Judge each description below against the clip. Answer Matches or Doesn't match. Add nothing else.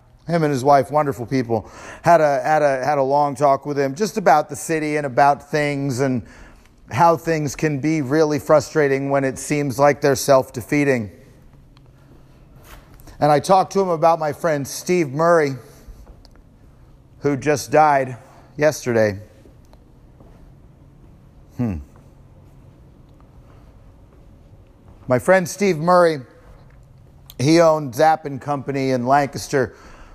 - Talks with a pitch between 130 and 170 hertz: Matches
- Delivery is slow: Matches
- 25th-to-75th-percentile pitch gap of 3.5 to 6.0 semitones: Doesn't match